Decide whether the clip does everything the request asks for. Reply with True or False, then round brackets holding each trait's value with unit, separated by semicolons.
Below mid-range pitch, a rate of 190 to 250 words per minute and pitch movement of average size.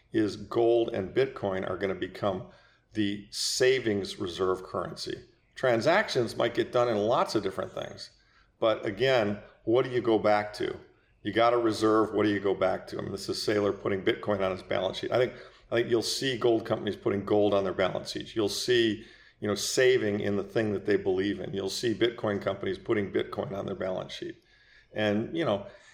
False (105 Hz; 205 wpm; 2.3 semitones)